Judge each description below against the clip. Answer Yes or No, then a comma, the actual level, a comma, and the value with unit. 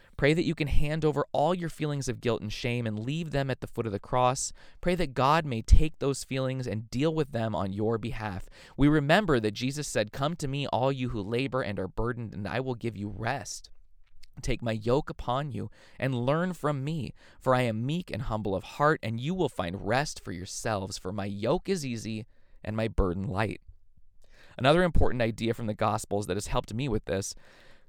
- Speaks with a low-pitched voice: Yes, low, 115 Hz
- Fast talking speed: Yes, fast, 220 wpm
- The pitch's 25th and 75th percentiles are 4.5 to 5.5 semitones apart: Yes, average, 5.1 semitones